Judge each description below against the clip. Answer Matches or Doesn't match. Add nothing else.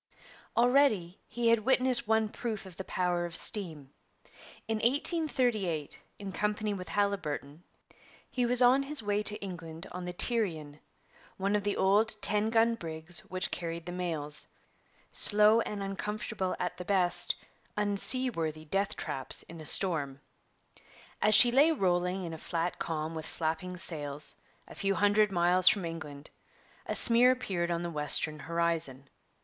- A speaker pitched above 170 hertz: Matches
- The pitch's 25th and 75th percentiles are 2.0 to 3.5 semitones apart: Doesn't match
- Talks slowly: Doesn't match